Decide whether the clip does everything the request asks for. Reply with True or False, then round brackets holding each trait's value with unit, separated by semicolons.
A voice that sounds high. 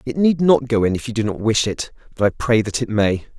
False (115 Hz)